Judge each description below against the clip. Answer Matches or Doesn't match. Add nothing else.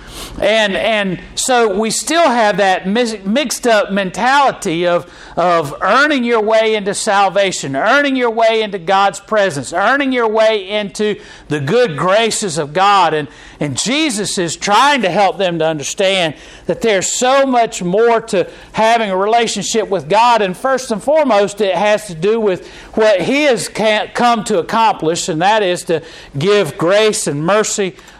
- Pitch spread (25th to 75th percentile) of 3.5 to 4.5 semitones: Matches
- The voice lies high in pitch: Matches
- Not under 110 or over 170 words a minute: Matches